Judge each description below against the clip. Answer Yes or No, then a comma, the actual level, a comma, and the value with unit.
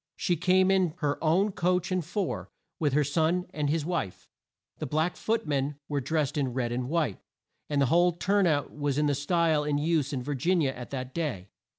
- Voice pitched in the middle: Yes, medium, 150 Hz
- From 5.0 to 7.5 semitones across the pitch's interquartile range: No, average, 3.7 semitones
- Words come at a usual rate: No, fast, 220 wpm